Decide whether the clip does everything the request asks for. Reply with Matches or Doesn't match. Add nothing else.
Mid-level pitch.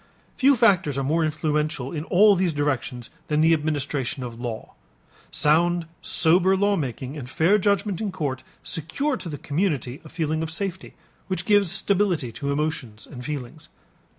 Matches